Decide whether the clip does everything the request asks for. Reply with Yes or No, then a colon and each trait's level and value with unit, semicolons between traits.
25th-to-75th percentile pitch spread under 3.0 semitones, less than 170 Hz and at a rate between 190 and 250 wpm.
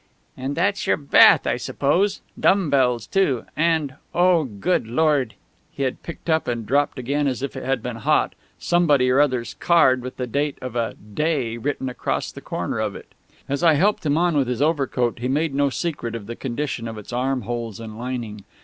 No: average, 4.2 semitones; low, 135 Hz; average, 200 wpm